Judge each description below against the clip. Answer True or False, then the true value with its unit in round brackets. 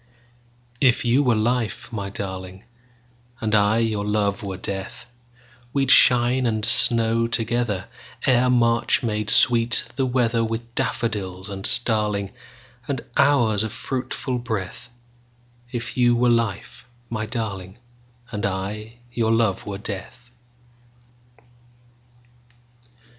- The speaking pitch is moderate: False (115 Hz)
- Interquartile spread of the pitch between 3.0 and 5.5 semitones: False (2.4 semitones)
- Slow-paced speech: True (95 wpm)